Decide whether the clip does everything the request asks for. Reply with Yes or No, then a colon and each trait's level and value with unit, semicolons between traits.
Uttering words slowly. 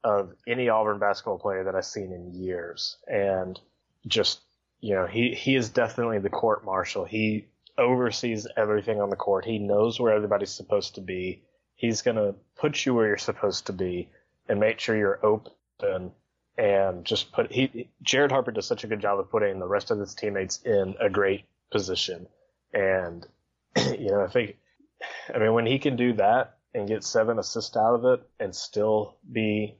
No: average, 185 wpm